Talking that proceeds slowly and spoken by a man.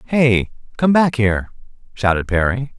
Yes: slow, 130 wpm; male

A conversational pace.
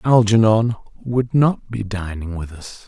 Yes: average, 145 wpm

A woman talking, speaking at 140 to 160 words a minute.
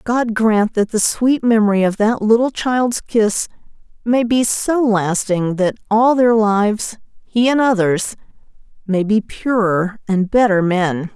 Yes: female; average, 150 wpm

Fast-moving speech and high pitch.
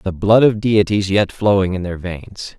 No: fast, 210 wpm; low, 100 Hz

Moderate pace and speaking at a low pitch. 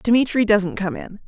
No: average, 190 wpm; high, 215 Hz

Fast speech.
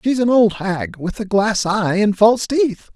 Yes: fast, 225 wpm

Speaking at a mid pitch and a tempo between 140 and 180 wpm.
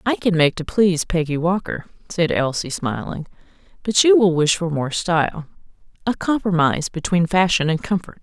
Yes: medium, 175 Hz; average, 160 wpm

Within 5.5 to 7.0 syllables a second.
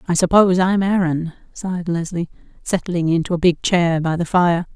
No: 5.2 syllables/s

